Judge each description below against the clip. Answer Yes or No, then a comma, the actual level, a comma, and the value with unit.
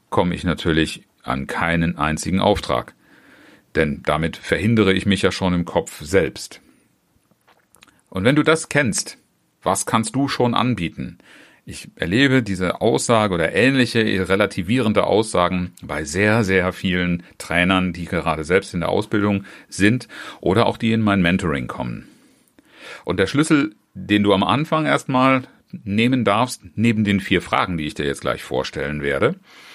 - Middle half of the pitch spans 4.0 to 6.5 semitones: Yes, average, 5.0 semitones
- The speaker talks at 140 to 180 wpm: Yes, average, 150 wpm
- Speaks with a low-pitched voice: Yes, low, 100 Hz